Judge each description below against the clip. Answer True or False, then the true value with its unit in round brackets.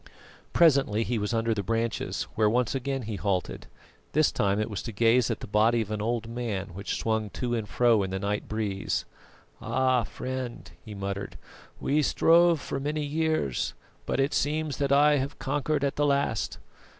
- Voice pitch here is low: True (115 Hz)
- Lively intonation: False (4.8 semitones)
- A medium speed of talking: True (185 wpm)